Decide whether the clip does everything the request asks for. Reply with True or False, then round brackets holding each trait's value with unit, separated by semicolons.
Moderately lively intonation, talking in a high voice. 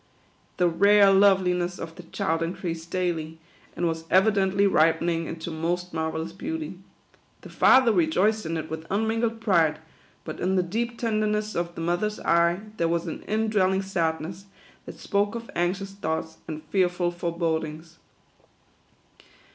False (3.4 semitones; 175 Hz)